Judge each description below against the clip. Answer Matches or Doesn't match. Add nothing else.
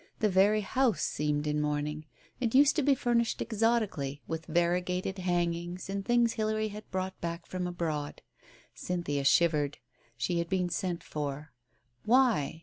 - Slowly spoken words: Doesn't match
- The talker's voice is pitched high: Doesn't match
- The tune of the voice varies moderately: Doesn't match